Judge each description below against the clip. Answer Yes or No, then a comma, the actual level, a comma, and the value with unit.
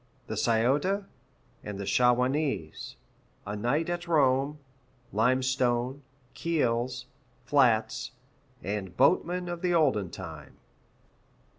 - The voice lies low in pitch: Yes, low, 130 Hz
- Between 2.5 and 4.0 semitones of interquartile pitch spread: No, average, 5.3 semitones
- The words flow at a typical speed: No, slow, 95 wpm